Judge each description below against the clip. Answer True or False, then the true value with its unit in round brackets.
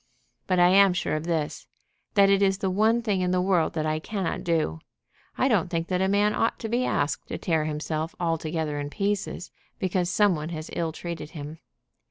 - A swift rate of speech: True (210 wpm)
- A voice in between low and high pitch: True (175 Hz)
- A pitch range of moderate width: True (3.9 semitones)